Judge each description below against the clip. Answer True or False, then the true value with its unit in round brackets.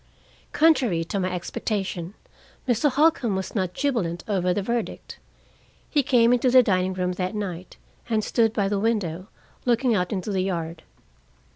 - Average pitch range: True (4.6 semitones)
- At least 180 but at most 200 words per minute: False (155 wpm)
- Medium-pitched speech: False (200 Hz)